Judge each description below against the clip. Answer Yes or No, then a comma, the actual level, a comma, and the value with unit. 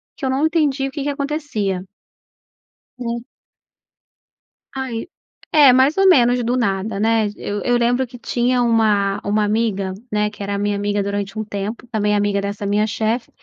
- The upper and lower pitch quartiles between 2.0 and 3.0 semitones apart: No, average, 3.8 semitones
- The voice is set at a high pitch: Yes, high, 225 Hz